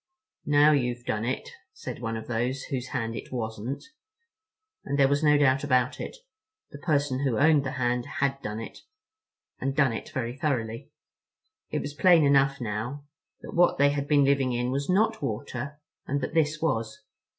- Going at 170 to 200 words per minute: Yes, average, 175 wpm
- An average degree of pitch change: Yes, average, 3.1 semitones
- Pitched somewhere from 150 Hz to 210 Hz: No, low, 135 Hz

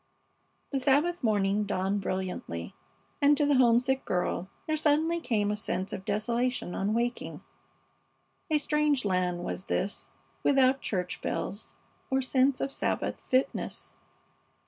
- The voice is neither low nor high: No, high, 240 Hz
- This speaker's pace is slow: Yes, slow, 130 wpm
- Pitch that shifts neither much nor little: No, wide, 6.0 semitones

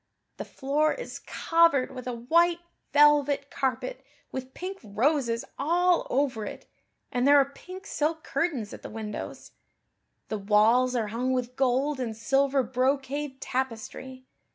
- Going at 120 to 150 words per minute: Yes, average, 140 wpm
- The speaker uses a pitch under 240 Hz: No, very high, 265 Hz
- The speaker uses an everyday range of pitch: Yes, average, 3.2 semitones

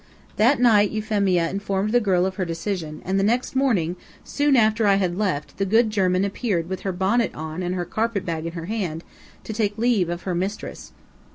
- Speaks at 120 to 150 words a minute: No, fast, 205 wpm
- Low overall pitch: No, high, 195 Hz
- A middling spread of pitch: Yes, average, 3.6 semitones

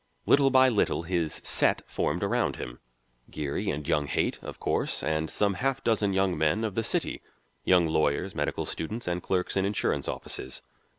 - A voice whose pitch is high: No, very low, 90 Hz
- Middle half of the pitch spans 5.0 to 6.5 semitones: Yes, wide, 5.4 semitones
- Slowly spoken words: No, average, 175 wpm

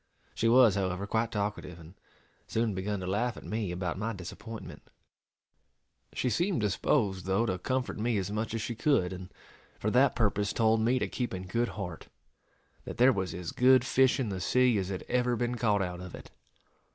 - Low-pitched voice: Yes, low, 105 Hz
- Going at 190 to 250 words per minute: Yes, average, 195 wpm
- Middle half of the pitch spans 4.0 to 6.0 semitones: Yes, average, 4.4 semitones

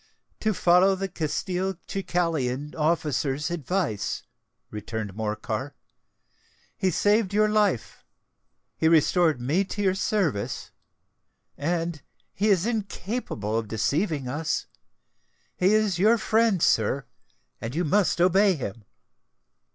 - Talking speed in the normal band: No, slow, 95 wpm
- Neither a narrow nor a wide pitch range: No, wide, 6.4 semitones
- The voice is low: No, medium, 170 Hz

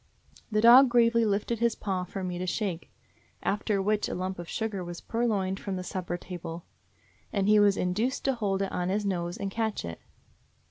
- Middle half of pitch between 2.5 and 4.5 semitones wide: Yes, average, 3.2 semitones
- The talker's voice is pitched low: No, high, 195 Hz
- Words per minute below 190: No, average, 200 wpm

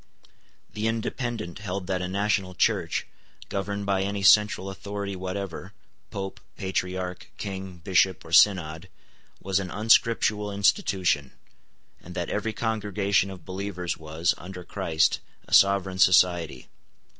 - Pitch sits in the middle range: No, very low, 95 Hz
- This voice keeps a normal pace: No, slow, 120 wpm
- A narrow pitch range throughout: Yes, narrow, 2.0 semitones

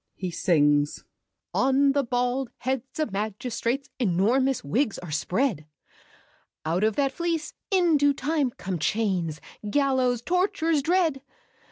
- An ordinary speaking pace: No, slow, 125 wpm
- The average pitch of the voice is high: Yes, very high, 255 Hz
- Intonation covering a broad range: Yes, wide, 6.6 semitones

